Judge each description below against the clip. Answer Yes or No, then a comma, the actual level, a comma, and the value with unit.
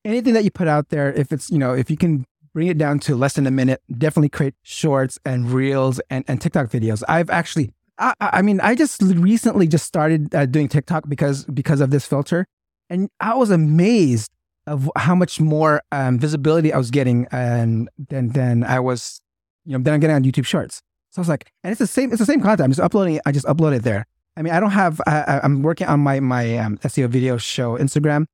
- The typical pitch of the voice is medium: Yes, medium, 145 Hz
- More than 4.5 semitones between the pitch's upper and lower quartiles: No, average, 4.0 semitones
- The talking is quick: Yes, fast, 235 wpm